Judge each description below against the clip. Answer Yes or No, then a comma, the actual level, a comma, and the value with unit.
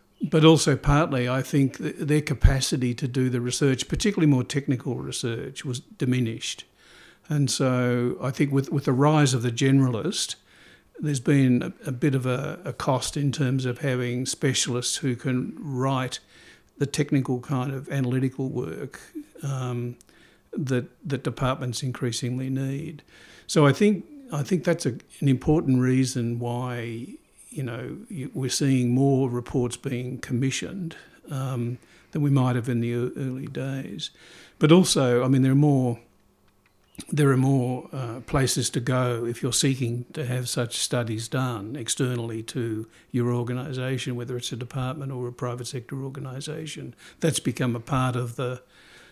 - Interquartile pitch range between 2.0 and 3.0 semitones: Yes, narrow, 2.5 semitones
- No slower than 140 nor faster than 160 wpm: Yes, average, 155 wpm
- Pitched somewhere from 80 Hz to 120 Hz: No, low, 130 Hz